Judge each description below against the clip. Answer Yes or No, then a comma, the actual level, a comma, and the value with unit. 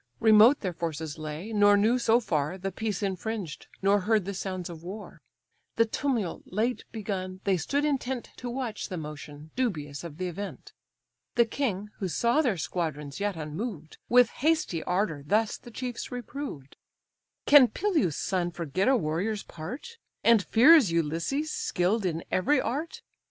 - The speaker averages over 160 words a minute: No, average, 155 wpm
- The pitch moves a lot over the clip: Yes, wide, 6.1 semitones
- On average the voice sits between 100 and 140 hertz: No, high, 200 Hz